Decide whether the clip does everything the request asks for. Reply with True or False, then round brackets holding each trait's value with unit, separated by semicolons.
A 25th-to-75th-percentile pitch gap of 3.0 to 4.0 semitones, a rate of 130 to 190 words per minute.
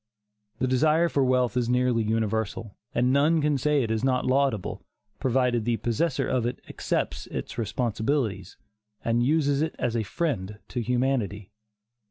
True (3.6 semitones; 155 wpm)